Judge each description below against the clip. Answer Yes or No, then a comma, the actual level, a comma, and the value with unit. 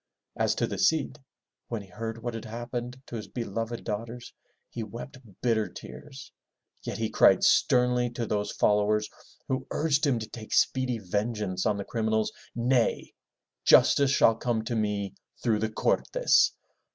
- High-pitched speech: No, low, 115 Hz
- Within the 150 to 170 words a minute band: Yes, average, 155 wpm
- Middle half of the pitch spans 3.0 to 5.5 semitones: No, narrow, 2.4 semitones